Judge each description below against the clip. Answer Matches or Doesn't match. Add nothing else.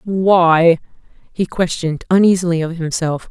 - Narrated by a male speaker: Doesn't match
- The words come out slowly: Matches